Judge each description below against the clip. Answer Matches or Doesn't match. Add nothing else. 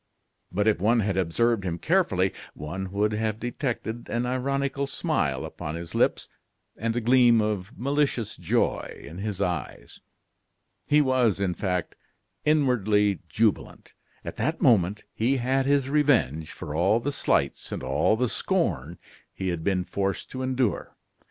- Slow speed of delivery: Doesn't match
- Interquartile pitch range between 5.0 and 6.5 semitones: Matches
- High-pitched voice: Doesn't match